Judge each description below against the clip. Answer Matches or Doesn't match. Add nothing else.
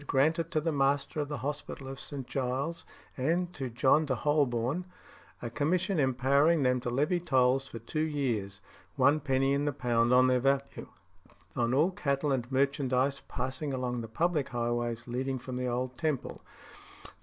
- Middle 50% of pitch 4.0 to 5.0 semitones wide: Doesn't match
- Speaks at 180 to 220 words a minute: Doesn't match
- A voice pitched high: Doesn't match